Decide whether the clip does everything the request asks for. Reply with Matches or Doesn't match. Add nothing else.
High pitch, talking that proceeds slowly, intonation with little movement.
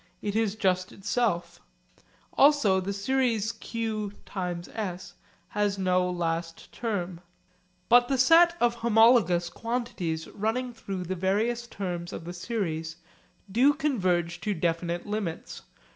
Doesn't match